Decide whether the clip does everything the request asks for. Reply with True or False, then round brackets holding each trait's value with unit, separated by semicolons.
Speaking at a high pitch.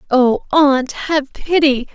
True (280 Hz)